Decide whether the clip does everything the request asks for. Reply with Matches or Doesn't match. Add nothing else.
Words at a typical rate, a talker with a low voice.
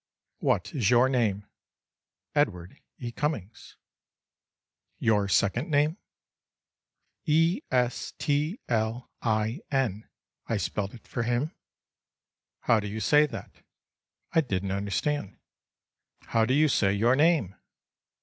Doesn't match